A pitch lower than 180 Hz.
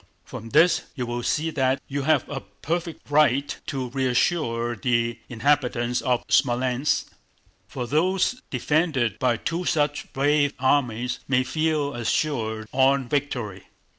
Yes: low, 135 Hz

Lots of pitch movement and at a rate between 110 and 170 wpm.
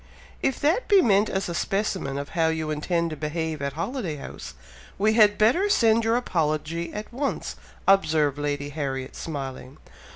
Yes: wide, 6.4 semitones; average, 165 wpm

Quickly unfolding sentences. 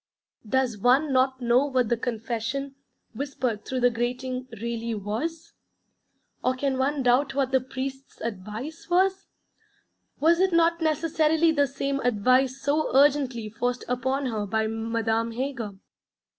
No: slow, 135 wpm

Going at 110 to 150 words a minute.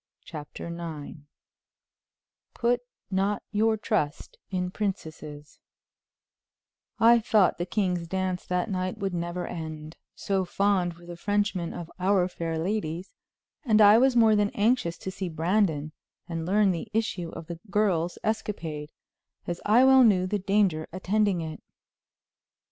Yes: slow, 135 wpm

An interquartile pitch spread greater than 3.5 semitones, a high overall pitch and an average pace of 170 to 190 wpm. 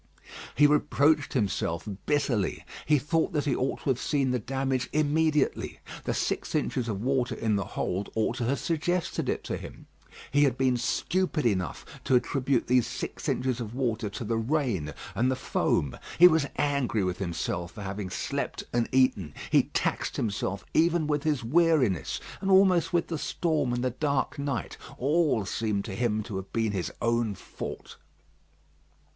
No: average, 5.3 semitones; low, 125 Hz; average, 175 wpm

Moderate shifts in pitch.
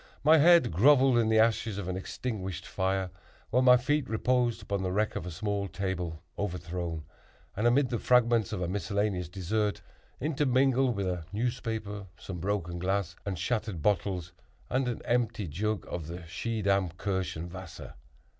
Yes: average, 4.7 semitones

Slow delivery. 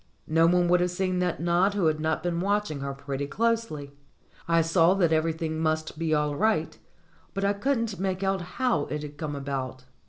No: average, 200 wpm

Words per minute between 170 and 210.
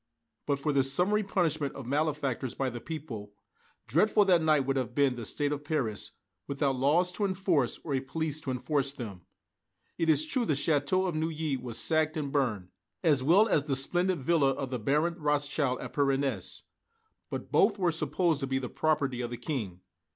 Yes: average, 190 wpm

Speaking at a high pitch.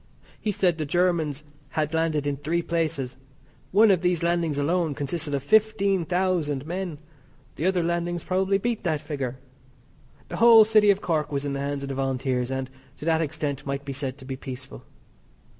No: medium, 160 Hz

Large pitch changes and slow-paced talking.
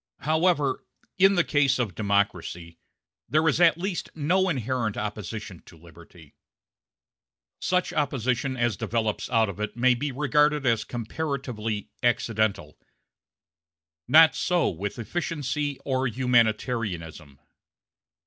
Yes: wide, 5.7 semitones; slow, 110 wpm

